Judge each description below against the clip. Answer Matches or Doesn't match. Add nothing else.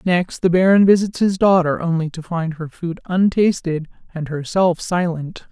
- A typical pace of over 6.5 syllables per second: Doesn't match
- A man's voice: Doesn't match